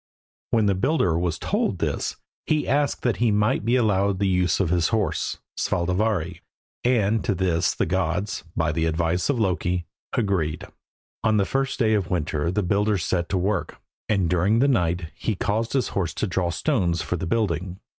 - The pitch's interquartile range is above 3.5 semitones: Yes, average, 3.9 semitones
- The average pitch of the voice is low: Yes, very low, 95 Hz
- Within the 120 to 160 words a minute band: No, average, 185 wpm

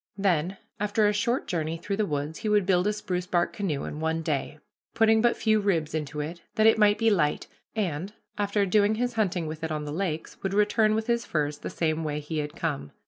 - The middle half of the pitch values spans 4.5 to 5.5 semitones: Yes, average, 5.1 semitones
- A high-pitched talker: No, medium, 180 Hz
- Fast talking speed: Yes, fast, 230 wpm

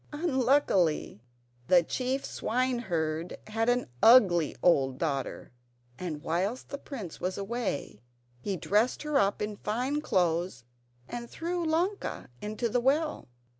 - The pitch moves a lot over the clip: Yes, wide, 7.0 semitones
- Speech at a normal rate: No, slow, 125 wpm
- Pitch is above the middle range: Yes, high, 215 Hz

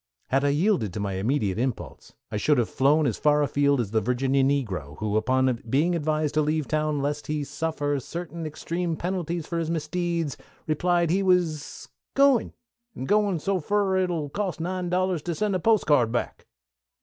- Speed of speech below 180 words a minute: No, average, 185 wpm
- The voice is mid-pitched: Yes, medium, 155 Hz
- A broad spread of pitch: No, average, 4.6 semitones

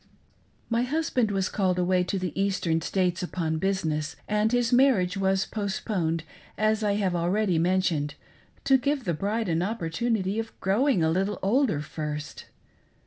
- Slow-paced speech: No, average, 150 wpm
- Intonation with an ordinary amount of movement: Yes, average, 4.1 semitones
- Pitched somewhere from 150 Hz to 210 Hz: Yes, high, 190 Hz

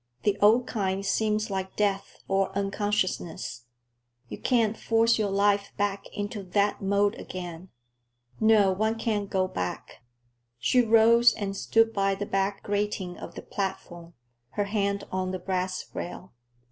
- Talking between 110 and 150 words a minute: Yes, average, 145 wpm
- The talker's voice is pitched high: Yes, high, 200 Hz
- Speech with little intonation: Yes, narrow, 1.9 semitones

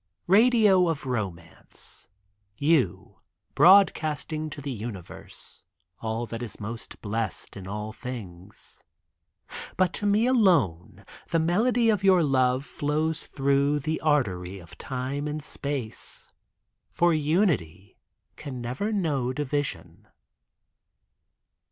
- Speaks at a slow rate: Yes, slow, 110 wpm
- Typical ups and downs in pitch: No, wide, 6.8 semitones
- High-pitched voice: No, medium, 140 Hz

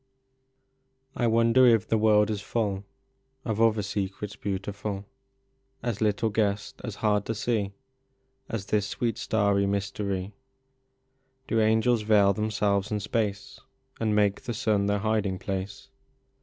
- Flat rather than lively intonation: Yes, narrow, 1.9 semitones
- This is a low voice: Yes, low, 105 Hz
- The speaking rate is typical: No, slow, 130 wpm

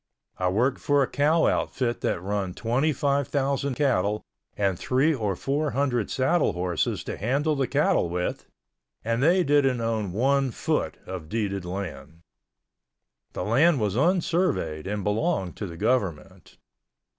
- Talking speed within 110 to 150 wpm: Yes, average, 145 wpm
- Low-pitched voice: Yes, low, 120 Hz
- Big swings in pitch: Yes, wide, 6.4 semitones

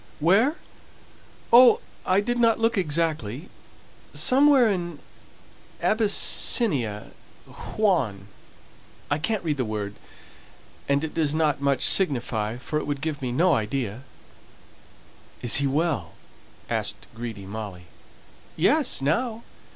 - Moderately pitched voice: Yes, medium, 150 Hz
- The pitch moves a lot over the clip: Yes, wide, 8.7 semitones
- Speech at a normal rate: No, slow, 105 wpm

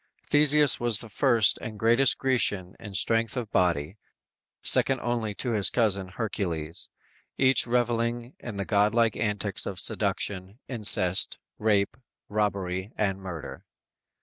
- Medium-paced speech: No, slow, 130 wpm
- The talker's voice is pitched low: Yes, low, 105 Hz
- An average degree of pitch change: Yes, average, 3.4 semitones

